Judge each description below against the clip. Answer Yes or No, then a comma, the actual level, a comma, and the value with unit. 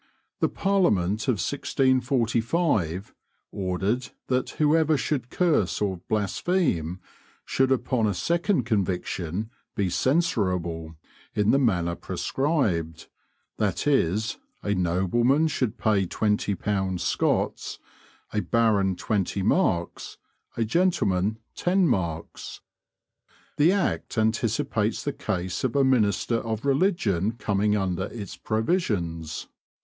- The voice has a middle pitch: No, low, 110 Hz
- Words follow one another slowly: Yes, slow, 105 wpm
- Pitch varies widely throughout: Yes, wide, 6.1 semitones